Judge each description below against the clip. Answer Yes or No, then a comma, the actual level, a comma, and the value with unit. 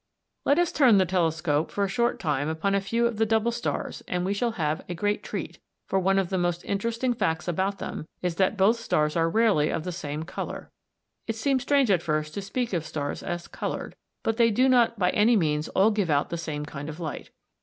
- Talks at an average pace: No, fast, 235 wpm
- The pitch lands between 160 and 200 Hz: Yes, high, 190 Hz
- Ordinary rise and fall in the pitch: No, wide, 5.7 semitones